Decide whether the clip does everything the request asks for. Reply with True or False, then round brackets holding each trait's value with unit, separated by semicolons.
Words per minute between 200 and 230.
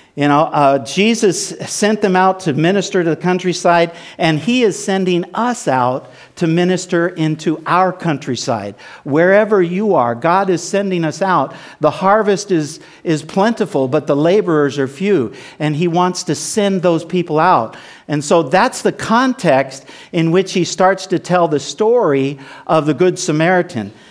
False (165 wpm)